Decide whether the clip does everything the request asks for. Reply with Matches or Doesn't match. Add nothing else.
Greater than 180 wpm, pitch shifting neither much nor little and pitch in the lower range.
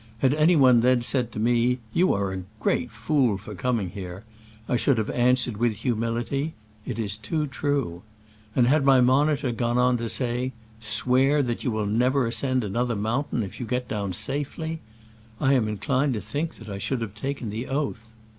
Matches